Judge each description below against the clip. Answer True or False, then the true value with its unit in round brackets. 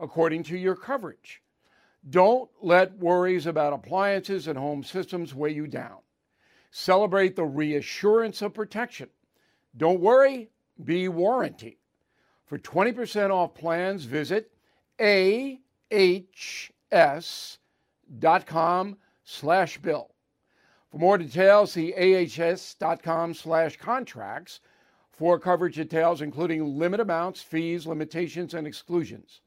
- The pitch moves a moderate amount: True (3.1 semitones)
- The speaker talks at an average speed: False (100 wpm)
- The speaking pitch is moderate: True (175 Hz)